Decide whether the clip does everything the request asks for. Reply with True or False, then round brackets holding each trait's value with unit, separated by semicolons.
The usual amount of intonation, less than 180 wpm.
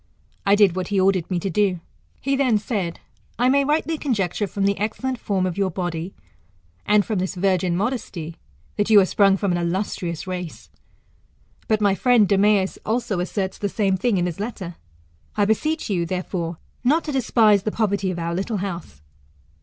False (3.1 semitones; 185 wpm)